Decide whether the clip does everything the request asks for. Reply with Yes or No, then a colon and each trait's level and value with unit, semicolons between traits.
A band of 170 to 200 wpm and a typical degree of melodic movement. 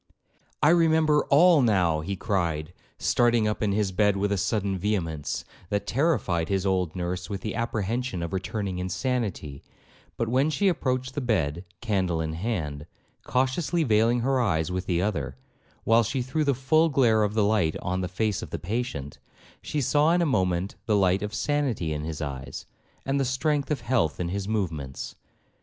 No: average, 185 wpm; wide, 6.2 semitones